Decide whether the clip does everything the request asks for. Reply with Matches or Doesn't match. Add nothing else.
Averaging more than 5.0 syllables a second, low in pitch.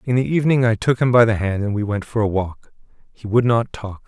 Matches